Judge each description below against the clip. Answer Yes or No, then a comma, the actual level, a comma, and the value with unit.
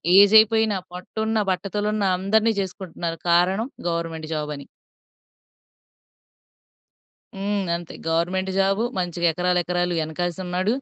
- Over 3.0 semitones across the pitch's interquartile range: No, average, 2.7 semitones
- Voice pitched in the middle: Yes, medium, 180 Hz